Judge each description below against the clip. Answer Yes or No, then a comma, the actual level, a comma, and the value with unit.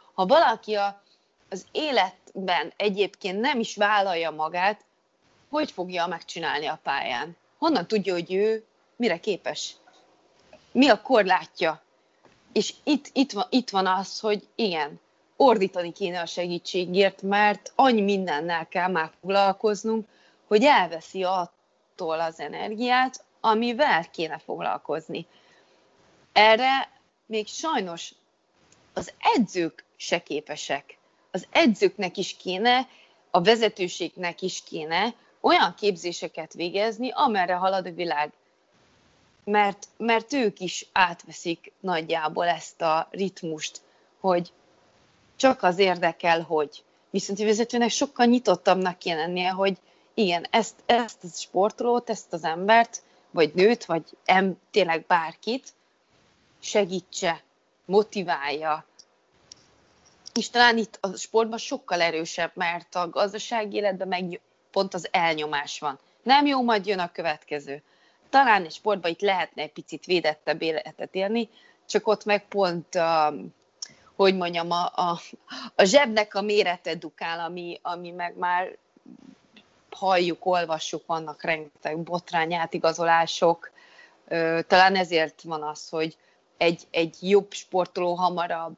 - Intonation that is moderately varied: Yes, average, 4.1 semitones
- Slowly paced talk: No, average, 120 wpm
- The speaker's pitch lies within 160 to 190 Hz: Yes, medium, 185 Hz